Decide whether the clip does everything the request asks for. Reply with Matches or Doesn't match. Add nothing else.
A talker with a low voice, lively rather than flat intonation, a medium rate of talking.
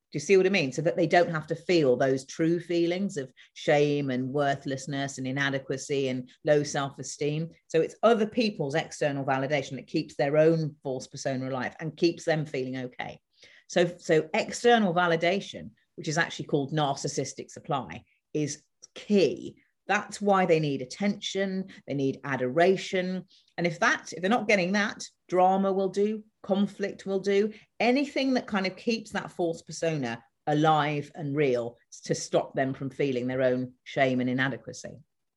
Doesn't match